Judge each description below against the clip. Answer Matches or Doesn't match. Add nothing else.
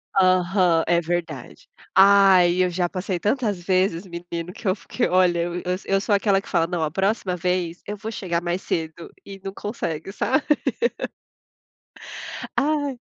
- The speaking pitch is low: Doesn't match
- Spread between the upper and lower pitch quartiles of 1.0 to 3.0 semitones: Matches